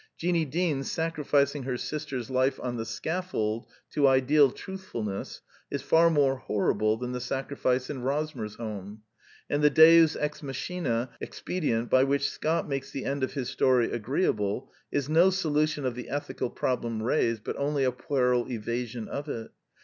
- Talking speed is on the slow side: No, average, 165 wpm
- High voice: No, low, 135 Hz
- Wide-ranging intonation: No, average, 3.8 semitones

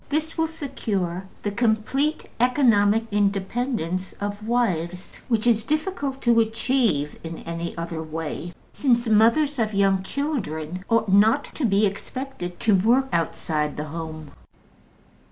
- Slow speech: Yes, slow, 130 wpm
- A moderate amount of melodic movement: No, wide, 6.0 semitones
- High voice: Yes, high, 215 Hz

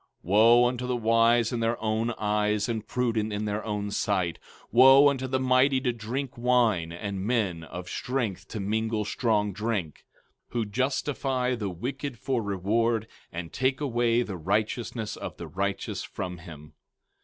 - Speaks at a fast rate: No, average, 165 wpm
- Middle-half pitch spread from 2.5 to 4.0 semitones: Yes, average, 3.4 semitones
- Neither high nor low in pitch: No, low, 110 Hz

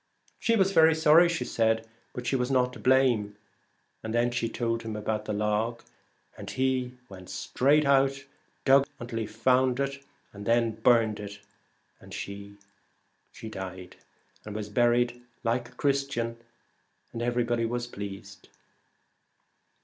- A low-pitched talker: Yes, low, 120 Hz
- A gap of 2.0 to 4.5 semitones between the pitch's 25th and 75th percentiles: Yes, average, 3.3 semitones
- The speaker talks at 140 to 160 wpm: Yes, average, 150 wpm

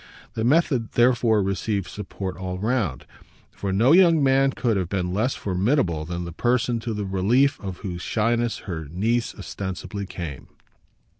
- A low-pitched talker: Yes, low, 105 Hz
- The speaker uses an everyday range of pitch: Yes, average, 4.6 semitones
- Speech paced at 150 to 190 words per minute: Yes, average, 155 wpm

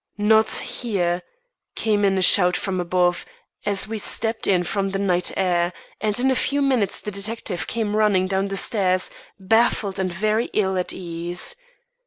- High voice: Yes, high, 195 Hz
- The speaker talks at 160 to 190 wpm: Yes, average, 170 wpm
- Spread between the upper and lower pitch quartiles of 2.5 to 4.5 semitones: Yes, average, 2.9 semitones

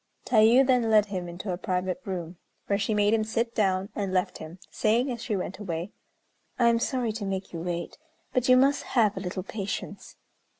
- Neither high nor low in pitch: No, high, 205 Hz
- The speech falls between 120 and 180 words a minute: No, fast, 205 wpm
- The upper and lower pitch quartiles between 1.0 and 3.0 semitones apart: No, average, 3.8 semitones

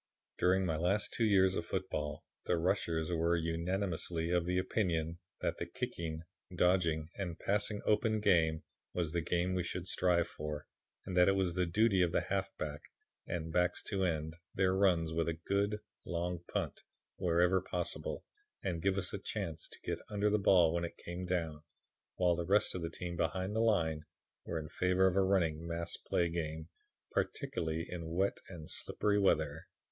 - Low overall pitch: Yes, very low, 90 Hz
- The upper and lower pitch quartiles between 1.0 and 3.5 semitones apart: Yes, narrow, 2.5 semitones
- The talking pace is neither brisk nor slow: Yes, average, 180 wpm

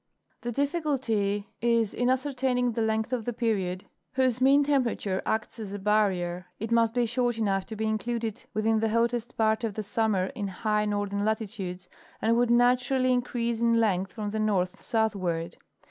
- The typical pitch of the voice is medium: No, high, 220 Hz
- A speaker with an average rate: Yes, average, 170 wpm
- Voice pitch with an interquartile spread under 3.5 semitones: Yes, average, 2.9 semitones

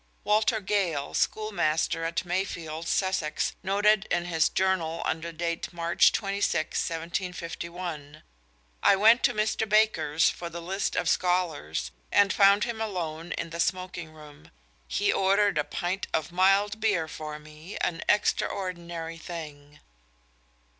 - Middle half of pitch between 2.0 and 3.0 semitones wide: No, average, 3.5 semitones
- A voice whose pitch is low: No, medium, 175 Hz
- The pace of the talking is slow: Yes, slow, 130 wpm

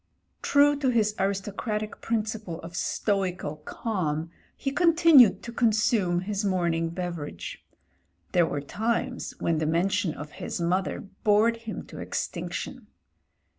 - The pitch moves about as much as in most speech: Yes, average, 5.0 semitones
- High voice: Yes, high, 200 Hz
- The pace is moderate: No, slow, 130 wpm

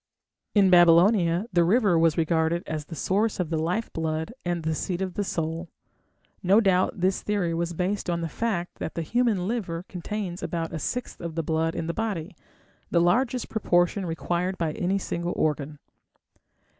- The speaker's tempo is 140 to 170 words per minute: No, average, 180 wpm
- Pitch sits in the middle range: Yes, medium, 175 Hz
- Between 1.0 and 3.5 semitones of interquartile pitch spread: Yes, average, 2.9 semitones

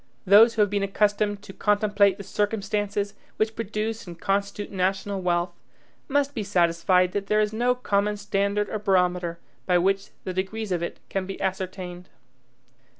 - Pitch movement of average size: No, narrow, 1.9 semitones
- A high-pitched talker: Yes, high, 200 Hz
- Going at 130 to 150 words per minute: No, average, 160 wpm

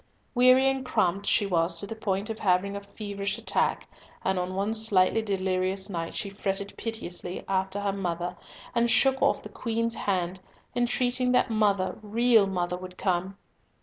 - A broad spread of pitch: No, average, 3.3 semitones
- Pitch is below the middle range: No, high, 200 Hz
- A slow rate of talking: No, average, 160 wpm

